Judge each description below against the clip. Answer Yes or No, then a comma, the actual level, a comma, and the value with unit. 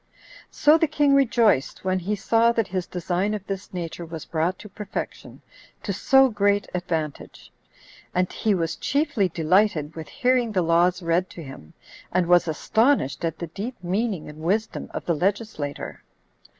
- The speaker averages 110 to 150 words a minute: No, average, 165 wpm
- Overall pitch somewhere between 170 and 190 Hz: Yes, medium, 185 Hz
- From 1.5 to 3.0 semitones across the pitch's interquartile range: No, average, 4.7 semitones